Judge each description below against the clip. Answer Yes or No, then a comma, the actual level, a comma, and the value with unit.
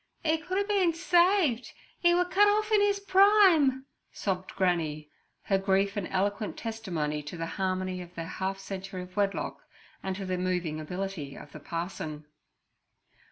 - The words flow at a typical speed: Yes, average, 160 wpm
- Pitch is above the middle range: Yes, high, 195 Hz